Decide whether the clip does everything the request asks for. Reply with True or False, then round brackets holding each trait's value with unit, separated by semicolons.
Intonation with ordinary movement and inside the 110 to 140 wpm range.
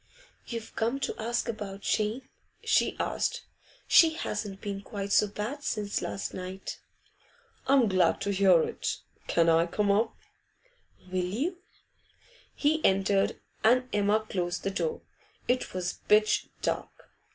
True (3.4 semitones; 135 wpm)